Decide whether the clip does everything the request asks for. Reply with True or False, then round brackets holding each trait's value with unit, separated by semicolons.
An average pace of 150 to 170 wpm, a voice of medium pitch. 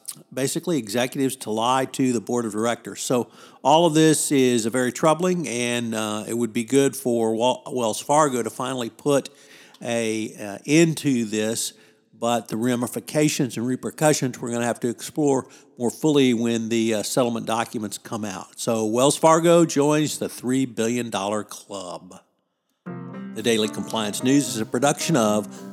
False (165 wpm; 120 Hz)